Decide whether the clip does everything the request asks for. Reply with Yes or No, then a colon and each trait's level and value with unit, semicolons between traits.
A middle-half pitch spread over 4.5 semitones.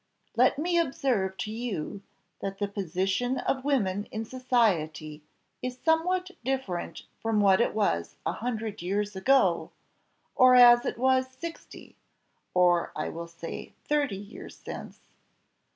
Yes: wide, 5.4 semitones